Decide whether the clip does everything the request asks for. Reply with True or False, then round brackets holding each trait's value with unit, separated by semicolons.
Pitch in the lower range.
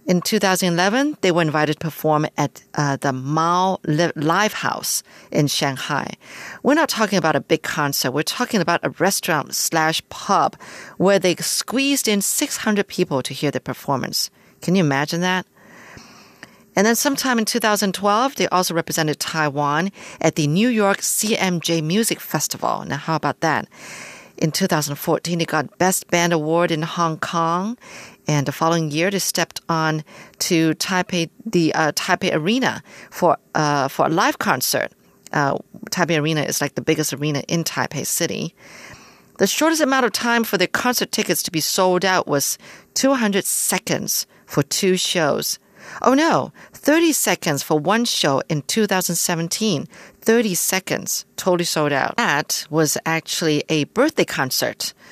False (170 Hz)